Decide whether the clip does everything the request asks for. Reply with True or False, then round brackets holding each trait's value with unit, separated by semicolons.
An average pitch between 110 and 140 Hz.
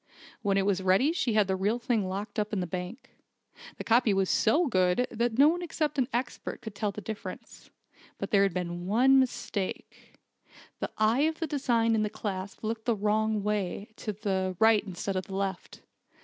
False (215 Hz)